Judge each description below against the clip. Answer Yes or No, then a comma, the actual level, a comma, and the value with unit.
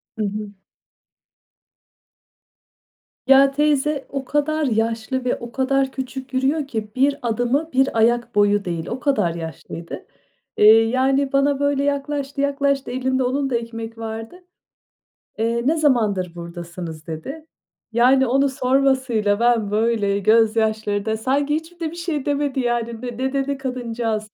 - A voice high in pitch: Yes, very high, 255 Hz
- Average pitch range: Yes, average, 3.8 semitones